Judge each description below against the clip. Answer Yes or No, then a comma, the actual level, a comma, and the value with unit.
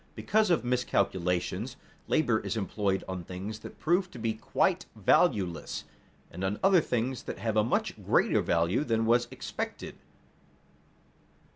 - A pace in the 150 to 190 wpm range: No, average, 140 wpm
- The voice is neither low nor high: No, low, 110 Hz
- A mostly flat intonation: No, average, 4.6 semitones